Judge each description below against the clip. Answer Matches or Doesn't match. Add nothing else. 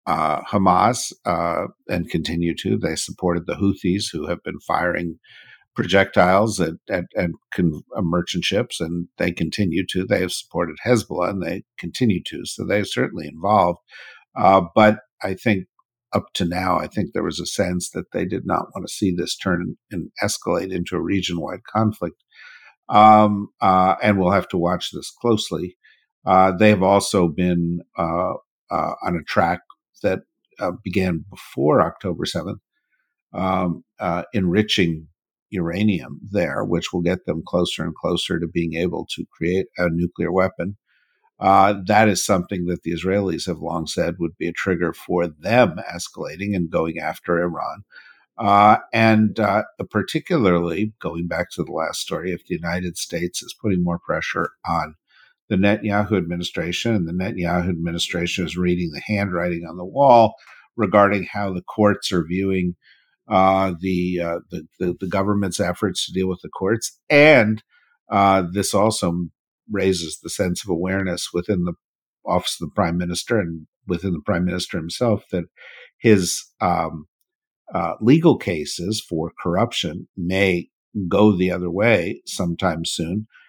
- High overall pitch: Doesn't match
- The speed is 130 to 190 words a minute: Matches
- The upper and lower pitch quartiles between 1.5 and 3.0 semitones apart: Matches